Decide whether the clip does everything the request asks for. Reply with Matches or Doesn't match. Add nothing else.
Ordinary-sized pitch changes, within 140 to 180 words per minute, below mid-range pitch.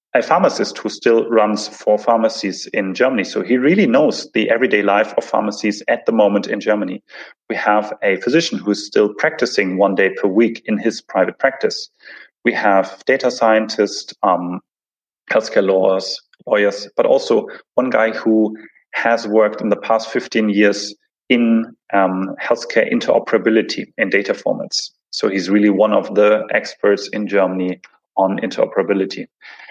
Doesn't match